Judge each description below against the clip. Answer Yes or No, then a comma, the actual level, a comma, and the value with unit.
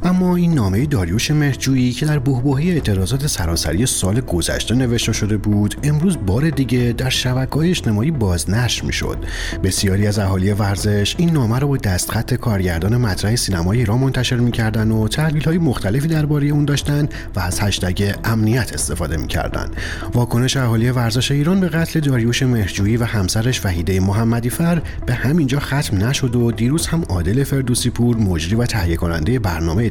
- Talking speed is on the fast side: Yes, fast, 160 wpm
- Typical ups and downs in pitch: No, wide, 5.8 semitones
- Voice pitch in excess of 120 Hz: No, low, 115 Hz